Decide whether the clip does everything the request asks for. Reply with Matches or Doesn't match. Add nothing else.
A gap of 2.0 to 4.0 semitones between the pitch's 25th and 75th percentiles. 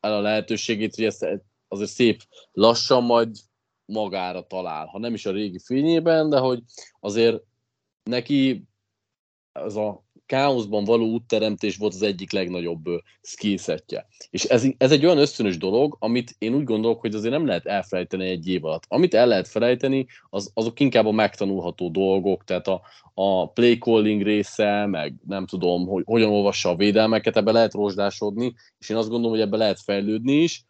Matches